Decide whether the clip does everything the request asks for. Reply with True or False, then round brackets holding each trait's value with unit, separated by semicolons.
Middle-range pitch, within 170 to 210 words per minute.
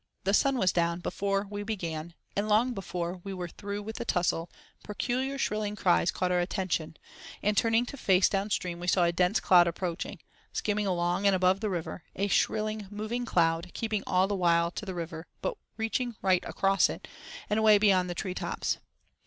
False (195 Hz; 190 wpm)